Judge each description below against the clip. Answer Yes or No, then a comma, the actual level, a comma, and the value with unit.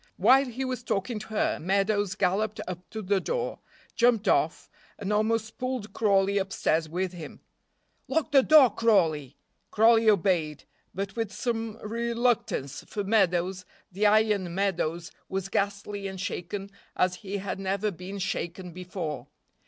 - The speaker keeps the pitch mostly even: No, average, 3.3 semitones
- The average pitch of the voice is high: Yes, high, 200 Hz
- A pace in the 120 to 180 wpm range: Yes, average, 145 wpm